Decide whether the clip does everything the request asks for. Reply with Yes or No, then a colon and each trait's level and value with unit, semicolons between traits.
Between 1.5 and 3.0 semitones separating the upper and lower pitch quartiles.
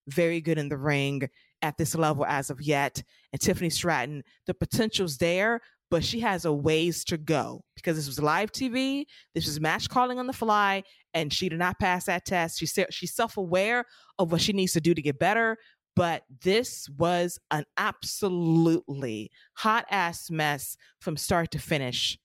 No: average, 4.1 semitones